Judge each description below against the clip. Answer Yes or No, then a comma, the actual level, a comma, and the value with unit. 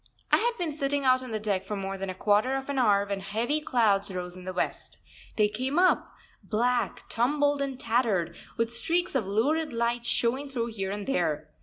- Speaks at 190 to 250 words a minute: Yes, fast, 205 wpm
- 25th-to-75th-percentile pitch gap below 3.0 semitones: No, average, 5.2 semitones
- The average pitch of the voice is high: Yes, high, 235 Hz